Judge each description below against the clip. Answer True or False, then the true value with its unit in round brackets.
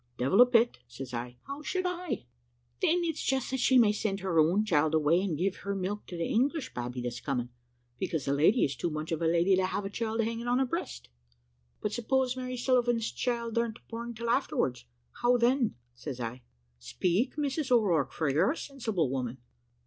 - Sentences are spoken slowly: False (200 wpm)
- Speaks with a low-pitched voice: False (210 Hz)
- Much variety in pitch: True (8.1 semitones)